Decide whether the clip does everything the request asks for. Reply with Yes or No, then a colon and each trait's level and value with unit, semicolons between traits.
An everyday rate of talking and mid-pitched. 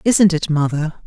Yes: average, 170 wpm; medium, 165 Hz